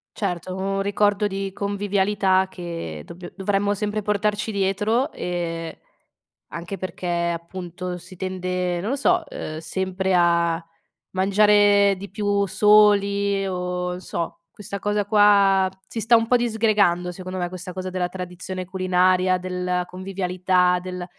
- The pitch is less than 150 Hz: No, high, 190 Hz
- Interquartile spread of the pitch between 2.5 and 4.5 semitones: No, narrow, 2.1 semitones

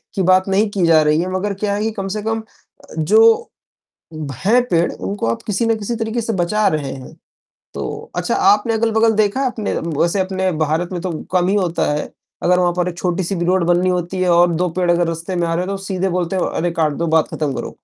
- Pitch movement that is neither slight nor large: Yes, average, 3.2 semitones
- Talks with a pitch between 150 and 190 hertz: Yes, medium, 185 Hz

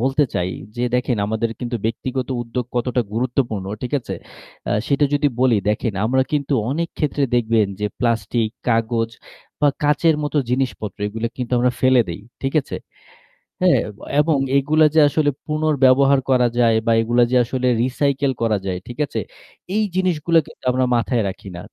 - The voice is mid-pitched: No, low, 125 Hz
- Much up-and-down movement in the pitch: No, average, 3.5 semitones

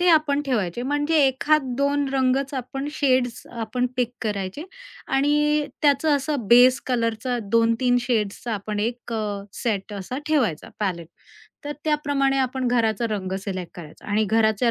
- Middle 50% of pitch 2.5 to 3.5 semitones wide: No, average, 4.5 semitones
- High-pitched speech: Yes, high, 245 Hz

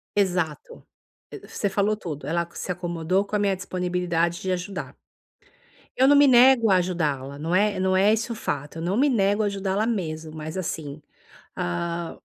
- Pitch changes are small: No, average, 3.7 semitones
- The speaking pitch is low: No, medium, 185 Hz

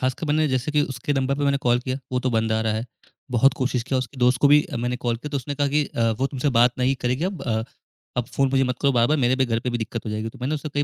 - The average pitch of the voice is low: Yes, low, 130 Hz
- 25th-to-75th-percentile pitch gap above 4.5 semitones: No, average, 2.7 semitones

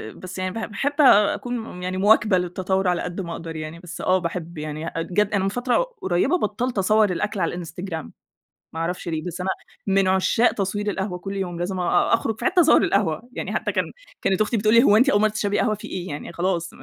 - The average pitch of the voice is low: No, high, 190 Hz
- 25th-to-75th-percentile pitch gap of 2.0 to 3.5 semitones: Yes, average, 3.2 semitones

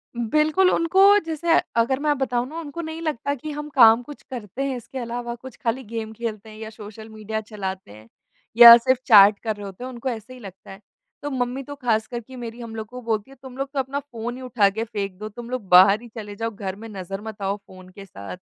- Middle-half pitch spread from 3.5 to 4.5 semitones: Yes, average, 3.8 semitones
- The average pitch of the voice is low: No, high, 230 Hz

